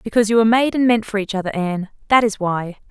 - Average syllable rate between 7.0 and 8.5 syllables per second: Yes, 7.1 syllables/s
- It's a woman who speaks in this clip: Yes, female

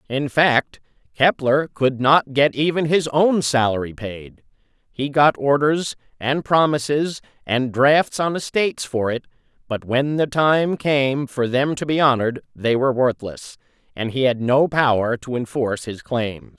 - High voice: No, low, 135 Hz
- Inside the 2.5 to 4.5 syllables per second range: Yes, 4.2 syllables/s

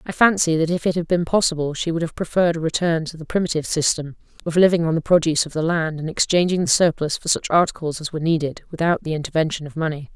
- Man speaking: No, female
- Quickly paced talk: Yes, fast, 240 wpm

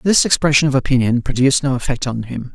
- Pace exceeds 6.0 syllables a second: Yes, 6.5 syllables/s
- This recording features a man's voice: Yes, male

